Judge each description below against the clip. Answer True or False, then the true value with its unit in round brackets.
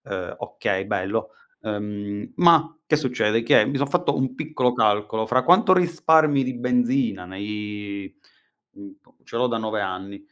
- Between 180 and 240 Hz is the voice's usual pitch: False (125 Hz)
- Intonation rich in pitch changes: True (7.4 semitones)